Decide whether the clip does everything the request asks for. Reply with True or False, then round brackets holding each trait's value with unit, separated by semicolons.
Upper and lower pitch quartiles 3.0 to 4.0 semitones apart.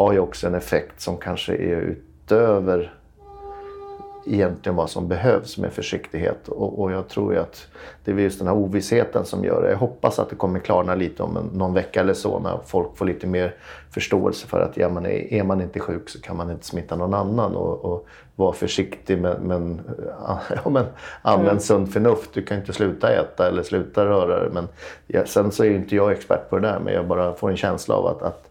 False (2.4 semitones)